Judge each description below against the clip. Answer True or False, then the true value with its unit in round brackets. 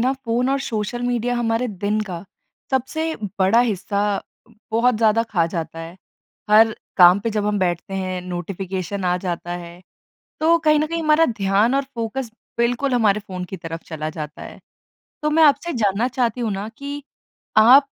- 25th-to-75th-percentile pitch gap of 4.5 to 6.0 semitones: True (5.1 semitones)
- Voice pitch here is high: True (215 Hz)